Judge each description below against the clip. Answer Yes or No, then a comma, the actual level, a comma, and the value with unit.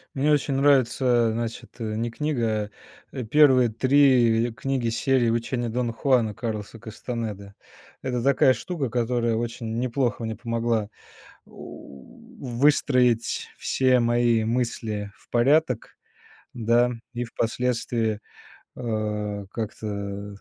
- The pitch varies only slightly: Yes, narrow, 2.3 semitones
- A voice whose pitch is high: No, low, 120 Hz